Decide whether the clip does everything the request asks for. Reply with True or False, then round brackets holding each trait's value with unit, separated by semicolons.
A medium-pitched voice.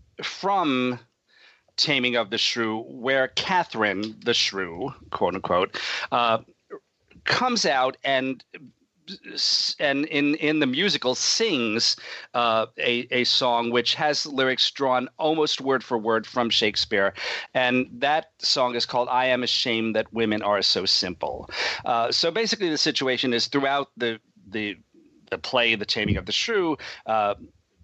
False (125 Hz)